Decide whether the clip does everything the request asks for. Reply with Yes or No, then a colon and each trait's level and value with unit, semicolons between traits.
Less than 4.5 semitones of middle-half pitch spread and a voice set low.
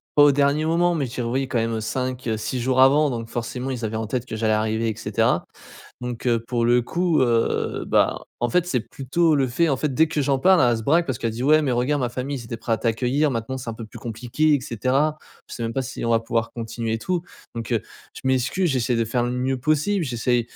Yes: average, 3.5 semitones; low, 125 Hz